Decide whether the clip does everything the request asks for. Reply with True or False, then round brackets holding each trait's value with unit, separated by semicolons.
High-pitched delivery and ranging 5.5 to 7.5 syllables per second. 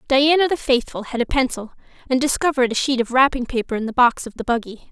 True (255 Hz; 6.5 syllables/s)